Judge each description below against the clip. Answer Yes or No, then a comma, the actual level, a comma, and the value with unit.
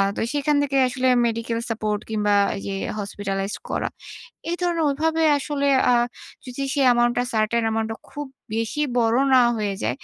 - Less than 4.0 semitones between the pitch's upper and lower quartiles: No, average, 4.4 semitones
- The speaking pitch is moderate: No, high, 235 Hz